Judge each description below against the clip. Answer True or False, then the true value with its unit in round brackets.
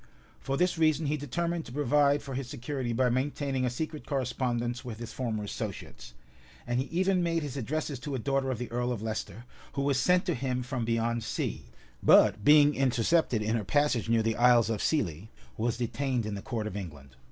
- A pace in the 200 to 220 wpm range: True (205 wpm)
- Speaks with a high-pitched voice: False (125 Hz)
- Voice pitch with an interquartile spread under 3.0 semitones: False (4.0 semitones)